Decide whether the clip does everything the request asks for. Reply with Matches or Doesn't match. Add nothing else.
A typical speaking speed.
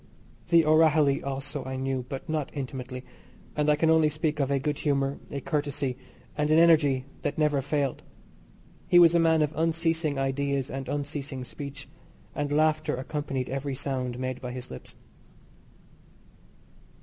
Matches